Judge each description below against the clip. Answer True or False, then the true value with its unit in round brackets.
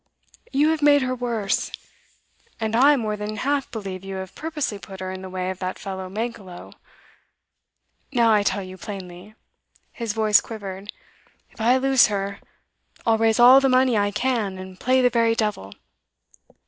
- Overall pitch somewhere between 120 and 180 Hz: False (215 Hz)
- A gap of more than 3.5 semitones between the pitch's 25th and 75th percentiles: True (4.4 semitones)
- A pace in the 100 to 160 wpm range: False (170 wpm)